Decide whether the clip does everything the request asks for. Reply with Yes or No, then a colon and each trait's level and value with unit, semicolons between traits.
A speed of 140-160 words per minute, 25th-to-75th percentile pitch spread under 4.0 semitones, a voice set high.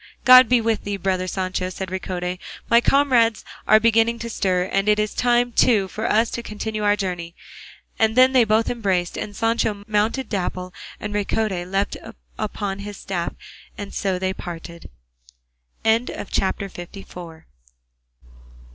Yes: average, 145 wpm; average, 3.5 semitones; high, 205 Hz